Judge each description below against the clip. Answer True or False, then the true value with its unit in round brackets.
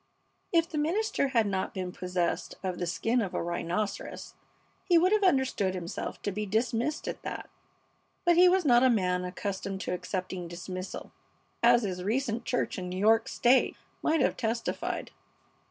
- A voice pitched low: False (215 Hz)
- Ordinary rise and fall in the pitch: False (6.2 semitones)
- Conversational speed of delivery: True (170 wpm)